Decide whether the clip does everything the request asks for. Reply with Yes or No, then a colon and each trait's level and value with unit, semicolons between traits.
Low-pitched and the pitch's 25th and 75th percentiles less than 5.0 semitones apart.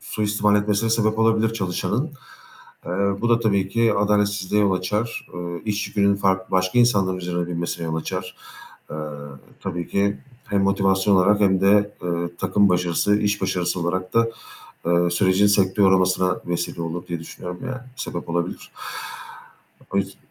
Yes: very low, 95 Hz; narrow, 2.5 semitones